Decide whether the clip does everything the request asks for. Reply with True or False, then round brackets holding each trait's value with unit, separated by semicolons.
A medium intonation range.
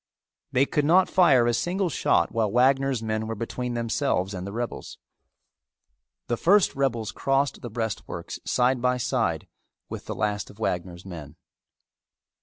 True (4.0 semitones)